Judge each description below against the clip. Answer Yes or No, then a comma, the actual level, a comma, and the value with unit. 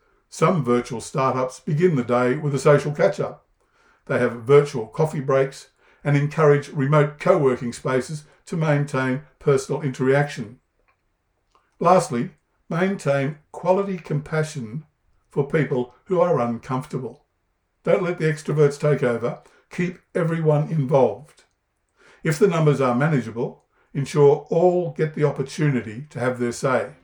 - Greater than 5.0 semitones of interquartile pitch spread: No, average, 3.4 semitones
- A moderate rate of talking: No, slow, 130 wpm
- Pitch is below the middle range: No, medium, 145 Hz